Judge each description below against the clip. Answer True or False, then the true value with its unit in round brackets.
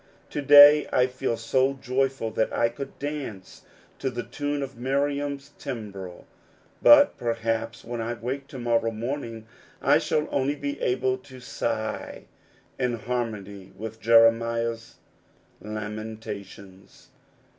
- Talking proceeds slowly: True (125 wpm)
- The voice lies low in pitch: True (120 Hz)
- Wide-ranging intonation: False (3.3 semitones)